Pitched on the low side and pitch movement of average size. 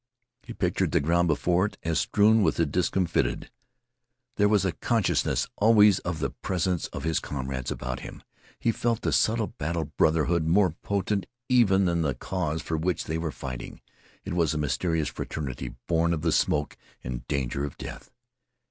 Yes: very low, 85 Hz; average, 4.2 semitones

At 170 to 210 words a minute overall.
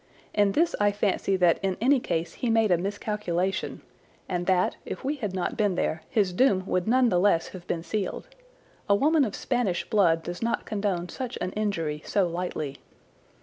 Yes: average, 190 wpm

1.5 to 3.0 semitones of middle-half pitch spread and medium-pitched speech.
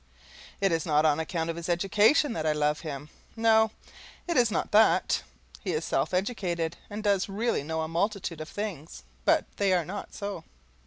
No: average, 4.5 semitones; medium, 175 Hz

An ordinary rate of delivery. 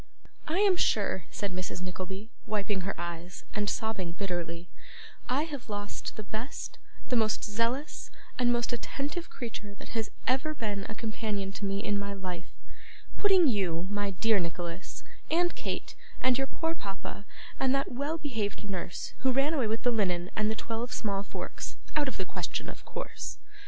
Yes: average, 170 wpm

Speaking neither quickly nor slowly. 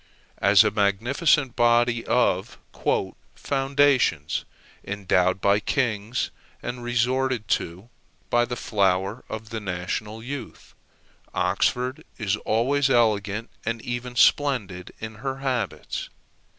No: slow, 105 wpm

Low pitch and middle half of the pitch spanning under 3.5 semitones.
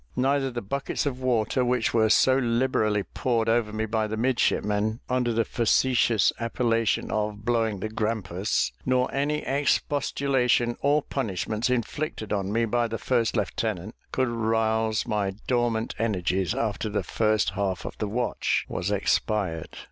Yes: low, 115 Hz; average, 2.8 semitones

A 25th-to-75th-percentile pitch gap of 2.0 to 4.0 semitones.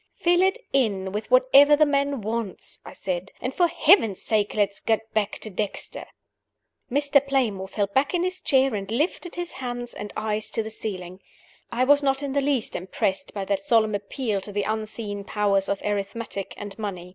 No: wide, 5.5 semitones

